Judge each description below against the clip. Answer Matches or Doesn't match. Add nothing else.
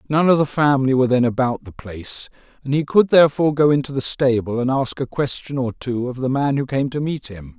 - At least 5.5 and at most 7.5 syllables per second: Matches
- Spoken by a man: Matches